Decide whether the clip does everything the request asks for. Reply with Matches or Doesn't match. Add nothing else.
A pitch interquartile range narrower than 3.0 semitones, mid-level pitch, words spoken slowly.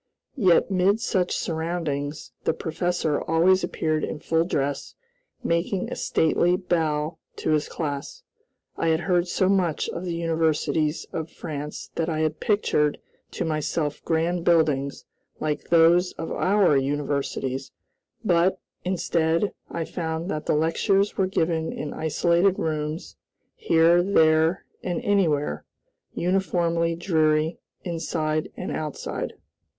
Matches